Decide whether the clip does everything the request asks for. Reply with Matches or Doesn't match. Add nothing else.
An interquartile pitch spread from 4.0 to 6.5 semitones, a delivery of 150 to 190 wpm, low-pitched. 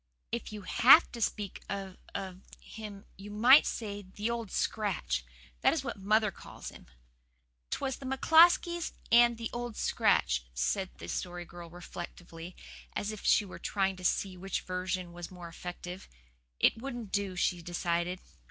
Doesn't match